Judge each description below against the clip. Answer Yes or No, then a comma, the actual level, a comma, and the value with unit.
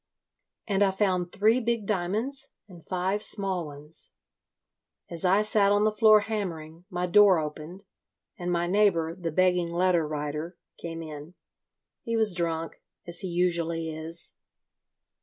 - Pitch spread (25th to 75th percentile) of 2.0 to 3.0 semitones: No, average, 3.7 semitones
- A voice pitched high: No, medium, 180 Hz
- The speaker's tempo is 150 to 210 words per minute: No, average, 140 wpm